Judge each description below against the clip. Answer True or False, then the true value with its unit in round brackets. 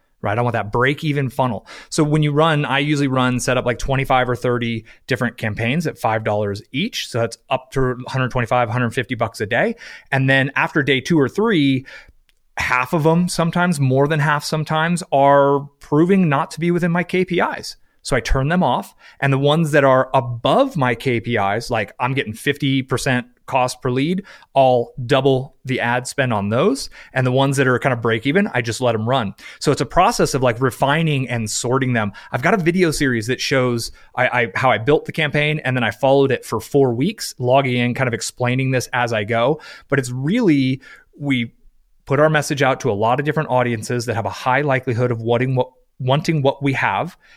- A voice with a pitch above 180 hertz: False (130 Hz)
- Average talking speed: False (210 wpm)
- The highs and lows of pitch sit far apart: False (3.0 semitones)